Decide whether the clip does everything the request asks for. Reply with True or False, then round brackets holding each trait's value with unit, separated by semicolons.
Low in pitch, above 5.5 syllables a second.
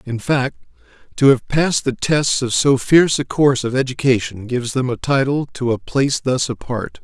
False (130 Hz; 5.2 syllables/s)